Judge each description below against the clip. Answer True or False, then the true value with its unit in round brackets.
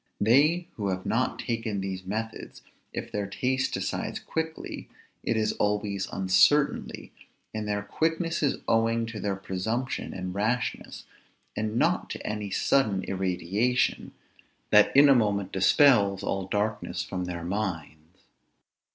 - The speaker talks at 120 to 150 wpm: True (135 wpm)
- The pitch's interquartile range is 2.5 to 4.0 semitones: True (3.6 semitones)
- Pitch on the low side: True (105 Hz)